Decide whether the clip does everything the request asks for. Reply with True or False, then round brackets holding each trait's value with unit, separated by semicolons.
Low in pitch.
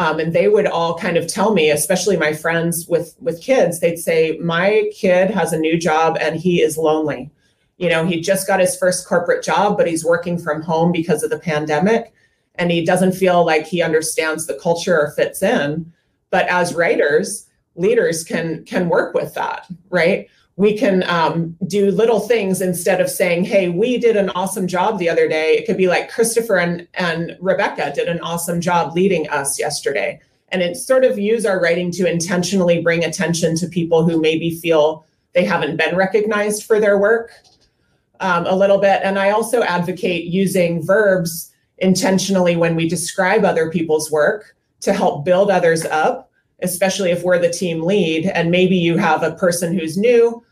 False (175 Hz)